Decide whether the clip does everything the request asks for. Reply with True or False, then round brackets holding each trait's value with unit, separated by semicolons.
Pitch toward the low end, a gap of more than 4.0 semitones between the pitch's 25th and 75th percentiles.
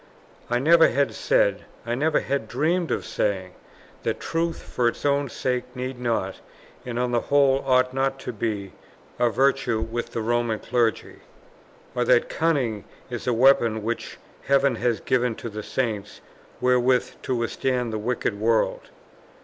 False (125 Hz; 2.9 semitones)